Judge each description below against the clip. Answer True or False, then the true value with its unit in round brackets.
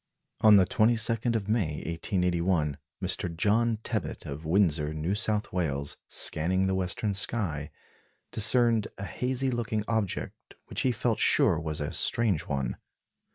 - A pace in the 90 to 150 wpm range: True (140 wpm)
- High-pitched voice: False (100 Hz)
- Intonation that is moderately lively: False (5.8 semitones)